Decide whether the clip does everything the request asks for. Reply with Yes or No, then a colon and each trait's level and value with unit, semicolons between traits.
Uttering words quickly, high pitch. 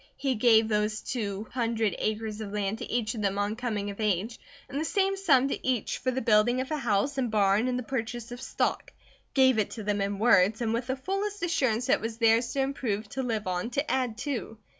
Yes: fast, 235 wpm; high, 230 Hz